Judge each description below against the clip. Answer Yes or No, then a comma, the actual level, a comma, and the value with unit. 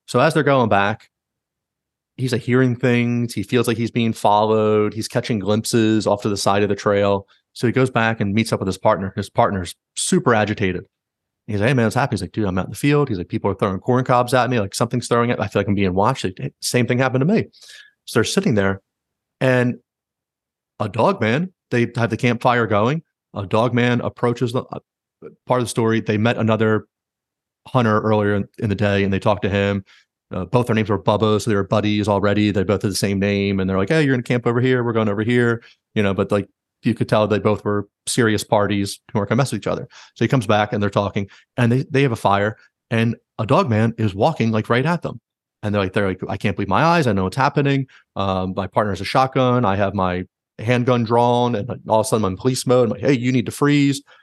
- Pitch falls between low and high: No, low, 110 Hz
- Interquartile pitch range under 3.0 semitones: No, average, 3.4 semitones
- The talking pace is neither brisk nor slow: No, fast, 250 wpm